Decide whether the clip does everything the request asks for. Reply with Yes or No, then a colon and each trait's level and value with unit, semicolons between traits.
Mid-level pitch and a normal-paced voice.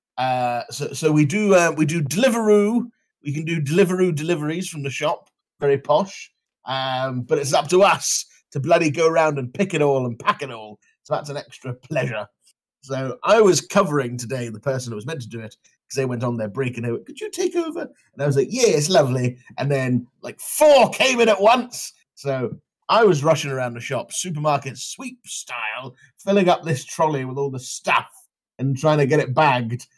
No: medium, 145 Hz; fast, 215 wpm